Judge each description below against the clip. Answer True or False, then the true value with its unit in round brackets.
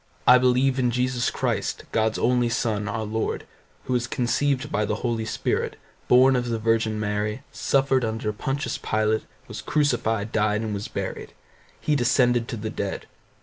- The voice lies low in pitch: True (115 Hz)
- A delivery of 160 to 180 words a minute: True (165 wpm)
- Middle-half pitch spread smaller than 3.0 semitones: True (2.6 semitones)